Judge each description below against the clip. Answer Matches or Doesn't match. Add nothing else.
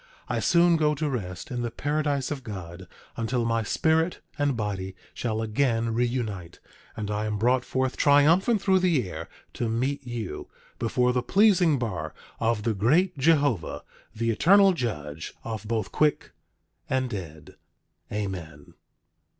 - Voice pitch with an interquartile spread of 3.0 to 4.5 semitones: Doesn't match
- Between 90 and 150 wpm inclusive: Matches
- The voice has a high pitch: Doesn't match